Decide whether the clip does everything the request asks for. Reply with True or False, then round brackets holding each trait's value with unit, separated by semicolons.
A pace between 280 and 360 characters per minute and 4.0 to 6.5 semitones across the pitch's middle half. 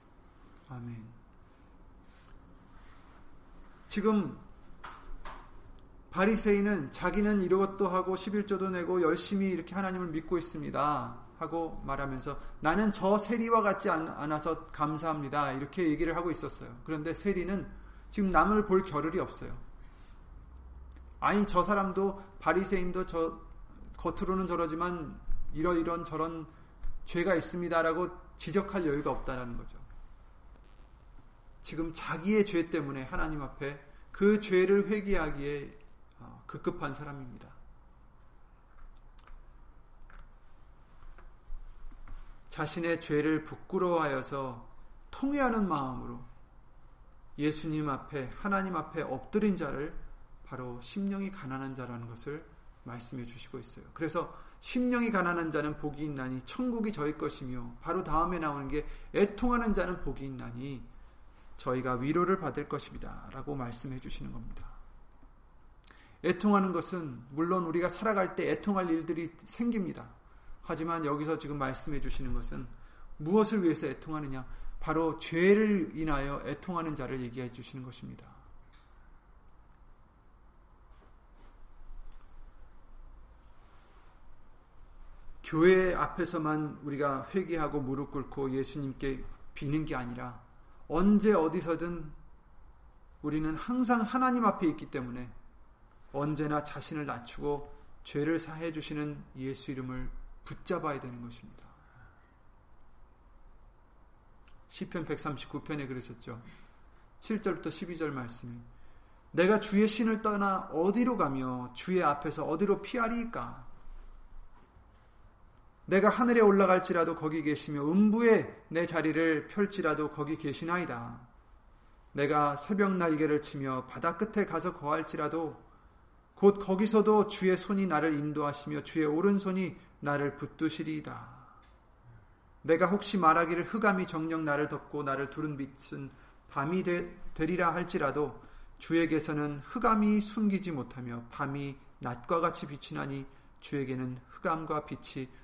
False (260 characters per minute; 5.3 semitones)